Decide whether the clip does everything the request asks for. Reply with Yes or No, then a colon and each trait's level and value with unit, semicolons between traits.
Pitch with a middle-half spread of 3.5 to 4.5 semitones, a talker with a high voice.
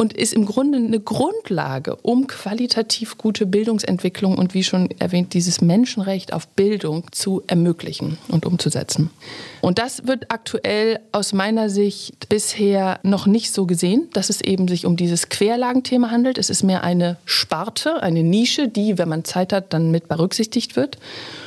Yes: average, 4.1 semitones; high, 200 Hz